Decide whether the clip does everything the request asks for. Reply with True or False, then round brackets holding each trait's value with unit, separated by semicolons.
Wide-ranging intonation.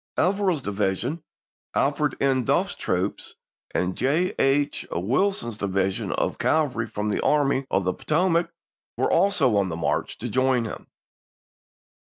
True (7.3 semitones)